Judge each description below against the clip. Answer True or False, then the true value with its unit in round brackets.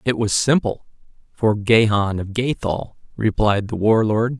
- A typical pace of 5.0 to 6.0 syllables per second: False (4.1 syllables/s)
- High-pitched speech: False (110 Hz)